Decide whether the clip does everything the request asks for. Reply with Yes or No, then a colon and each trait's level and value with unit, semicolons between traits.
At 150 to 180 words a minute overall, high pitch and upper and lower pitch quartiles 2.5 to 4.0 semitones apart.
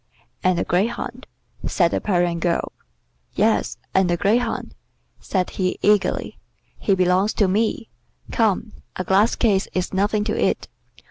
No: average, 140 wpm; high, 195 Hz; average, 2.8 semitones